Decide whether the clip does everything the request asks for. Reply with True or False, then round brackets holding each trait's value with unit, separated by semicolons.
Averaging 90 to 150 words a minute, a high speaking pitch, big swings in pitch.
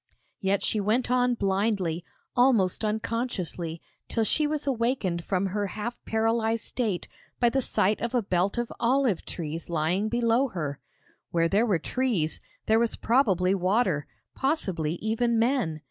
False (145 wpm; 215 Hz; 4.7 semitones)